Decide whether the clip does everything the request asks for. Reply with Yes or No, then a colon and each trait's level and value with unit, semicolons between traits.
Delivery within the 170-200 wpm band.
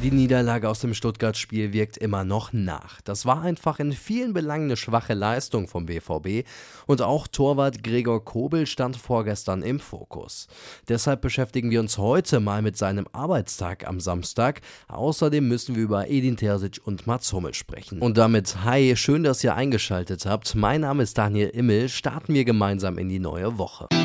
Yes: average, 175 wpm